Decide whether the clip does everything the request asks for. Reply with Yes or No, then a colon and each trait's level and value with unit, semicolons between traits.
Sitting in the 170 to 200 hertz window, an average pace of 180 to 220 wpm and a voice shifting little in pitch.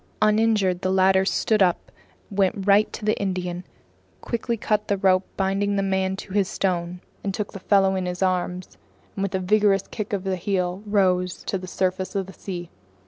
Yes: high, 190 Hz; average, 190 wpm; narrow, 1.6 semitones